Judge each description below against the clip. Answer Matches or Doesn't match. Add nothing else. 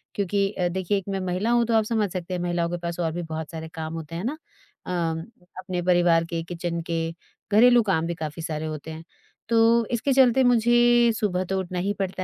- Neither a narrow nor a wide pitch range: Matches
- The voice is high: Doesn't match